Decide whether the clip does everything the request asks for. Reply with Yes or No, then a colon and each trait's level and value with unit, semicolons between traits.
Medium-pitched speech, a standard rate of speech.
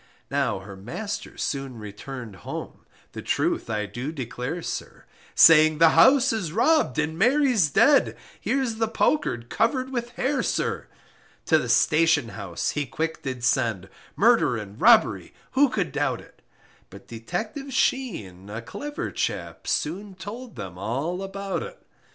Yes: medium, 160 Hz; average, 145 wpm